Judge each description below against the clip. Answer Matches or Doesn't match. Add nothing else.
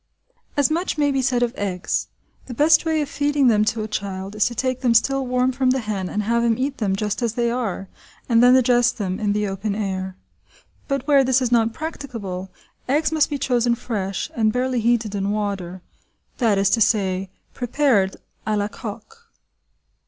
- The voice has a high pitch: Matches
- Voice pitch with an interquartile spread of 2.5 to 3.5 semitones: Doesn't match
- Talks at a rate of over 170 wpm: Matches